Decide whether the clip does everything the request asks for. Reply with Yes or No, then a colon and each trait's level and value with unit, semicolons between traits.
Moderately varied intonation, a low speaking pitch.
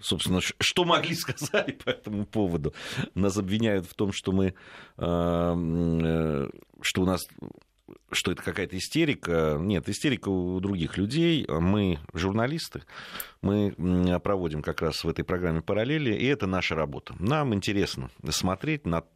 Yes: average, 3.9 semitones; very low, 95 Hz